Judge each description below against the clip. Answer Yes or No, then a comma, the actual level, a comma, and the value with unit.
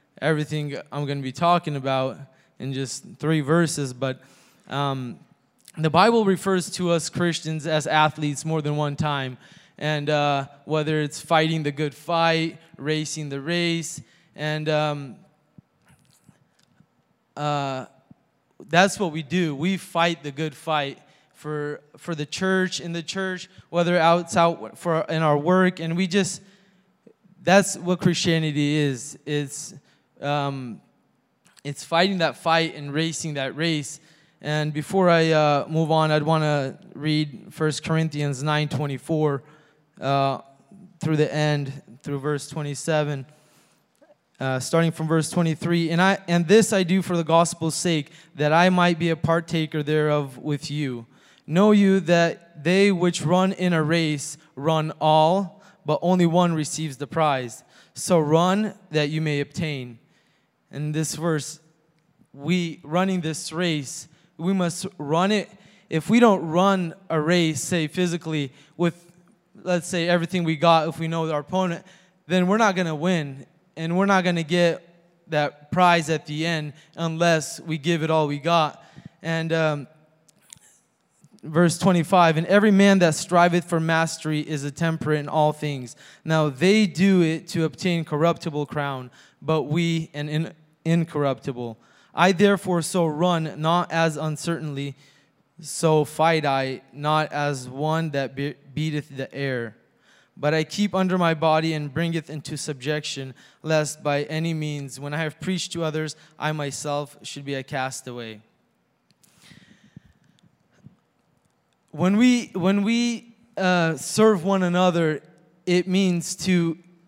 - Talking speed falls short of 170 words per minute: Yes, average, 145 wpm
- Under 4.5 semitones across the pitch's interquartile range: Yes, average, 2.8 semitones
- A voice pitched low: No, medium, 160 Hz